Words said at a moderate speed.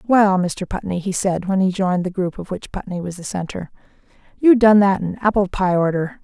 No: fast, 220 wpm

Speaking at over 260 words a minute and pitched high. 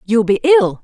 No: fast, 215 wpm; high, 240 Hz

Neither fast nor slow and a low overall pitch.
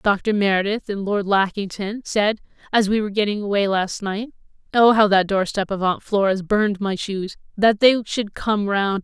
No: average, 175 wpm; high, 205 Hz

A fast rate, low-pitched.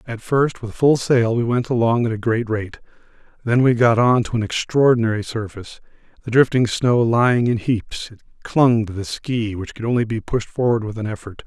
Yes: fast, 210 wpm; low, 115 Hz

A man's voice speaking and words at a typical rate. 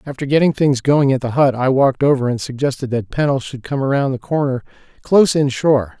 No: male; fast, 220 wpm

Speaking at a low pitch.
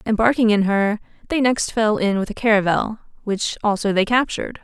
No: high, 215 Hz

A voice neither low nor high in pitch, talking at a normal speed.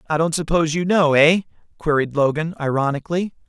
Yes: medium, 160 Hz; average, 155 wpm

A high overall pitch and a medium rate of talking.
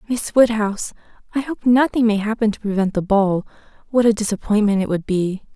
Yes: high, 215 Hz; average, 185 wpm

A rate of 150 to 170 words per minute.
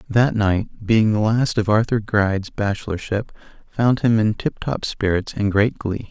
Yes: average, 165 wpm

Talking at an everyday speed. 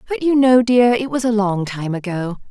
No: fast, 240 wpm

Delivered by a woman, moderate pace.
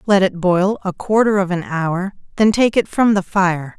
No: female; fast, 220 wpm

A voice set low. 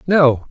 No: medium, 145 Hz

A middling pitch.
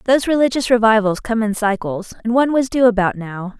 No: high, 225 Hz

